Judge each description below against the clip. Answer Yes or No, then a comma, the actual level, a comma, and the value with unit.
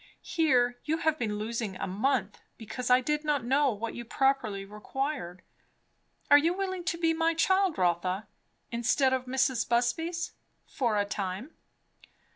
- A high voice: Yes, very high, 255 Hz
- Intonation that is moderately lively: No, wide, 6.1 semitones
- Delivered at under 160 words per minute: Yes, average, 150 wpm